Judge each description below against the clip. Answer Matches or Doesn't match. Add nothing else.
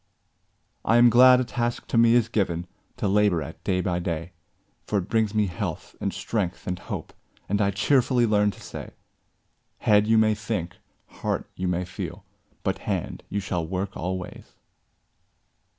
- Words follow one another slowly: Doesn't match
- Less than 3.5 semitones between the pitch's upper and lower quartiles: Doesn't match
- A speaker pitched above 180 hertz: Doesn't match